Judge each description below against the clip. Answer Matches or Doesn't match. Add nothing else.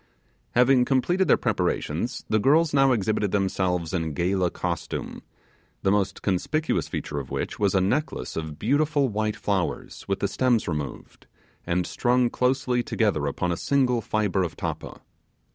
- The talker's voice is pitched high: Doesn't match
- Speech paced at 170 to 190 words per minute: Doesn't match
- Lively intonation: Matches